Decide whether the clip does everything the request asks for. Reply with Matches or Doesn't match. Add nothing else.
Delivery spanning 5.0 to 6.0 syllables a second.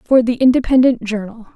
Matches